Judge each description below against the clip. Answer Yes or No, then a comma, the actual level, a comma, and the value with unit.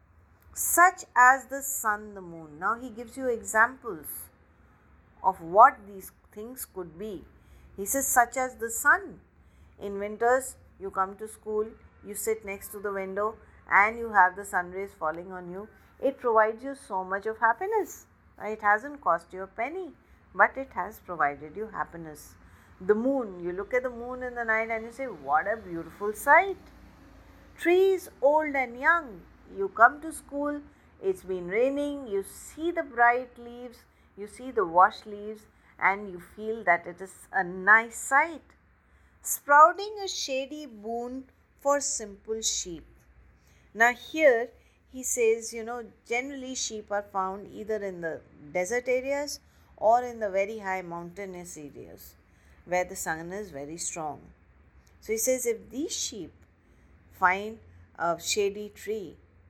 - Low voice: No, high, 220 Hz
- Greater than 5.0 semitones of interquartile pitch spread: Yes, wide, 5.6 semitones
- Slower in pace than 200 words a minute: Yes, average, 155 wpm